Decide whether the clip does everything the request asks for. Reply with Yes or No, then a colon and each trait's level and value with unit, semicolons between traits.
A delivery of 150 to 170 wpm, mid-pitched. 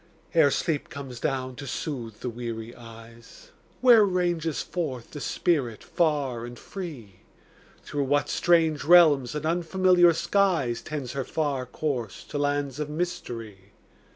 No: slow, 135 wpm; medium, 145 Hz